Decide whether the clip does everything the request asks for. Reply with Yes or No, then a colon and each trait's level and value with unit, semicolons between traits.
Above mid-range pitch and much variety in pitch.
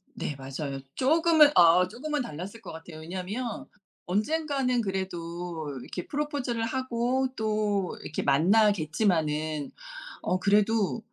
Yes: high, 200 Hz; wide, 6.8 semitones